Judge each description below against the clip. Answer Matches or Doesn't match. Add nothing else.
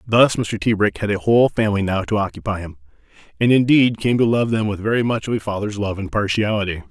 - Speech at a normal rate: Doesn't match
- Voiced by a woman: Doesn't match